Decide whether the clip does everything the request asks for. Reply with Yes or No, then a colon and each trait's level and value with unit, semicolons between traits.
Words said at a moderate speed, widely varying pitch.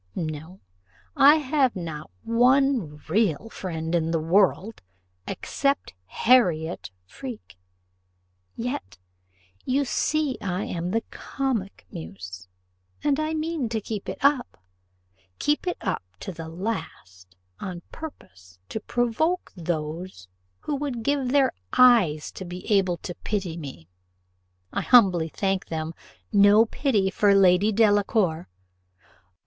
No: slow, 120 wpm; wide, 7.4 semitones